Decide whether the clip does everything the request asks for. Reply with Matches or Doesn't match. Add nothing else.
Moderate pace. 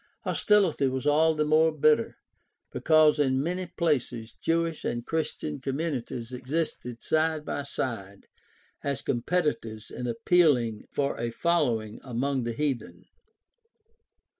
Doesn't match